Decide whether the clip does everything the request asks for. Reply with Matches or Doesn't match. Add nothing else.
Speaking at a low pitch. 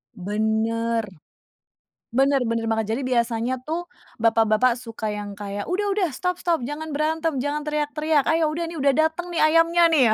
Doesn't match